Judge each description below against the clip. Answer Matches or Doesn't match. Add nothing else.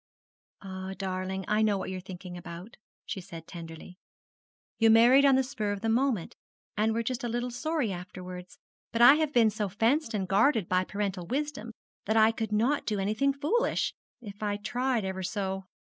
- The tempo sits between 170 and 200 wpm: Matches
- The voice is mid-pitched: Doesn't match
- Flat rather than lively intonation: Doesn't match